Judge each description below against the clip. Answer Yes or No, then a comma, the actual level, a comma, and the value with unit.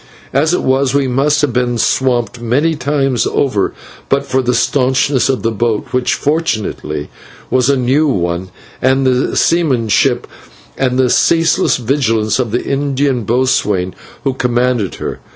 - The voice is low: Yes, low, 130 Hz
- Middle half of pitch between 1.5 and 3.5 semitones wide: Yes, average, 2.9 semitones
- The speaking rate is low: No, average, 145 wpm